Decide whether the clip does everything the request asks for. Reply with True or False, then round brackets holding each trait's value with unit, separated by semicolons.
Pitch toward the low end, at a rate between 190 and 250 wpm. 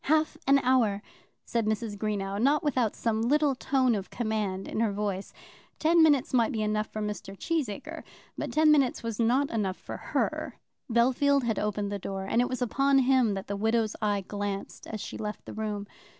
False (225 Hz; 195 wpm)